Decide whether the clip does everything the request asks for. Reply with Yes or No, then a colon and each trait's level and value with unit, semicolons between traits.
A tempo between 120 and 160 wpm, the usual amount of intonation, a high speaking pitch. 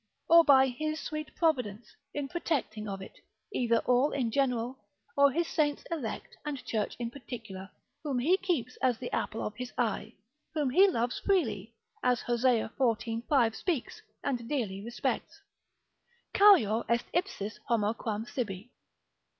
Yes: average, 150 wpm; average, 4.5 semitones; high, 245 Hz